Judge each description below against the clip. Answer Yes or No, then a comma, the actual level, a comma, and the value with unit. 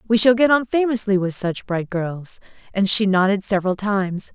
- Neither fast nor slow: Yes, average, 195 wpm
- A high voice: Yes, high, 205 Hz